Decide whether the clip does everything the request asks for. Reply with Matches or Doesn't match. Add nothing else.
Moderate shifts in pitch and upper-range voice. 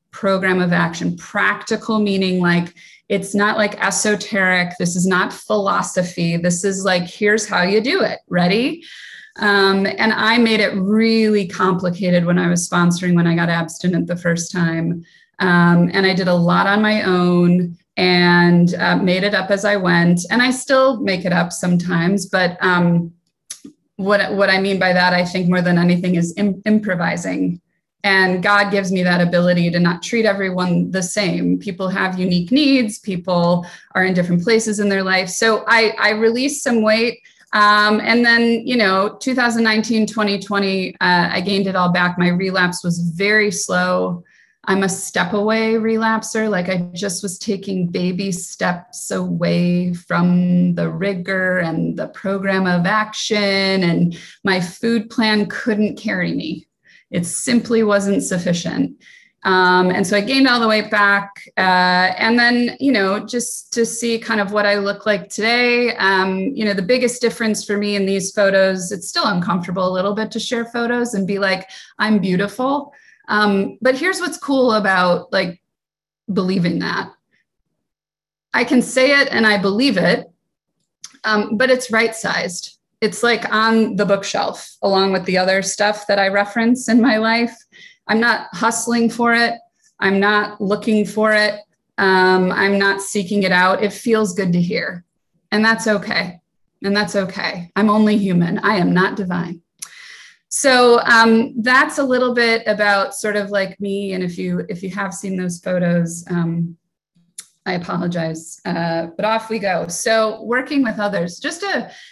Matches